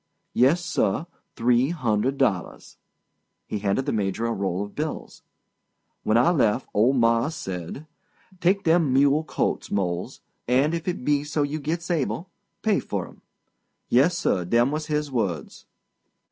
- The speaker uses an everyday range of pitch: No, wide, 6.4 semitones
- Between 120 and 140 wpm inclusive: Yes, slow, 135 wpm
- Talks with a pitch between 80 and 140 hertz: Yes, low, 135 Hz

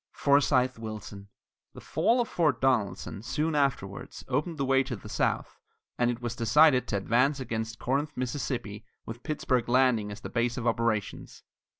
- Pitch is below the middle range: Yes, low, 125 Hz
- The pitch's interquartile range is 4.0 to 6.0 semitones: No, average, 3.6 semitones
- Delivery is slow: No, average, 165 wpm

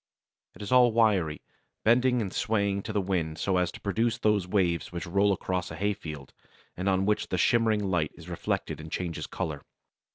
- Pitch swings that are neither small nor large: Yes, average, 3.6 semitones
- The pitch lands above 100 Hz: No, very low, 95 Hz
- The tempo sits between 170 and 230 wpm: Yes, average, 195 wpm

